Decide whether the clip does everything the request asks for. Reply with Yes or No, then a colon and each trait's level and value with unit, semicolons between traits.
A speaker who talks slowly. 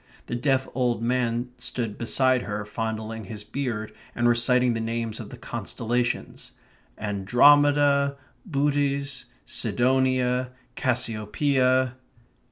Yes: slow, 100 wpm